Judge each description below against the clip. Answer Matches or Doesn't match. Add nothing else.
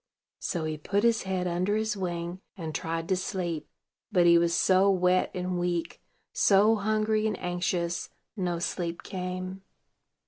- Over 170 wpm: Doesn't match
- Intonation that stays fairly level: Matches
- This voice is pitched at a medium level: Matches